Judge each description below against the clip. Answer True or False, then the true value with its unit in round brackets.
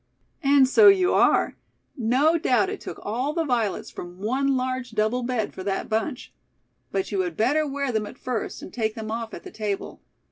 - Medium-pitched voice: False (250 Hz)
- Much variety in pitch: False (4.5 semitones)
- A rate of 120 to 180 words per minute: False (200 wpm)